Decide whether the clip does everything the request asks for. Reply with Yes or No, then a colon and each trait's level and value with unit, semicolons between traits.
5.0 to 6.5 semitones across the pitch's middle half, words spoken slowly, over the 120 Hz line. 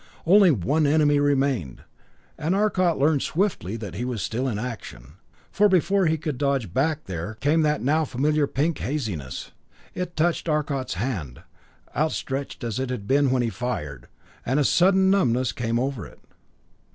No: average, 5.3 semitones; average, 165 wpm; medium, 140 Hz